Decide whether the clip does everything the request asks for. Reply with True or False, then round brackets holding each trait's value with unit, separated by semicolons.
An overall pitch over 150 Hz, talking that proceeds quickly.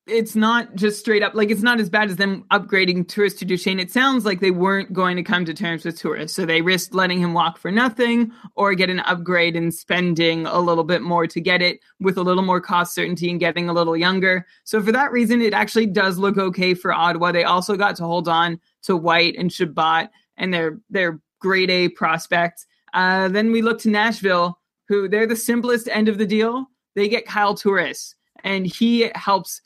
True (190 Hz; 220 wpm)